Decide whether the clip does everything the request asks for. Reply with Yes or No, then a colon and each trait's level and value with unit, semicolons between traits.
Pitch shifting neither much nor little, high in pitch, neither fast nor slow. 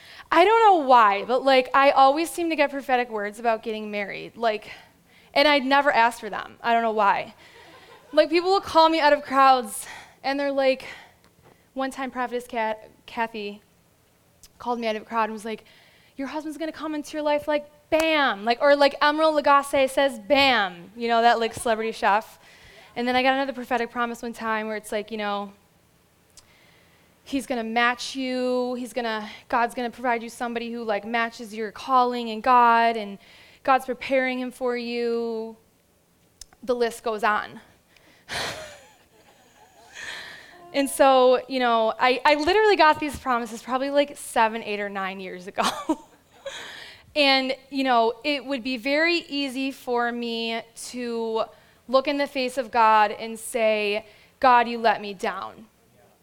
Yes: average, 3.6 semitones; high, 245 Hz; average, 170 wpm